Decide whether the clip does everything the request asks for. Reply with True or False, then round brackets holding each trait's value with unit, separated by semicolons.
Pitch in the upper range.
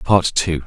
False (85 Hz)